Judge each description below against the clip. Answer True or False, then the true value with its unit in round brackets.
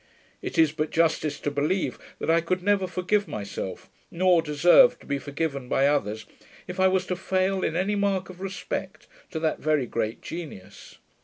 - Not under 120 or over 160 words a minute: False (180 wpm)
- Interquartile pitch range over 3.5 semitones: True (4.2 semitones)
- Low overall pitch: False (170 Hz)